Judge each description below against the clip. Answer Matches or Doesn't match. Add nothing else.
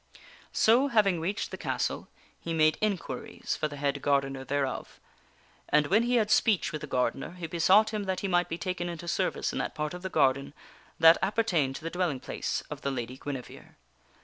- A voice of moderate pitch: Matches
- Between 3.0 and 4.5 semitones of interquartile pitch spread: Doesn't match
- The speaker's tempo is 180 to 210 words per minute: Matches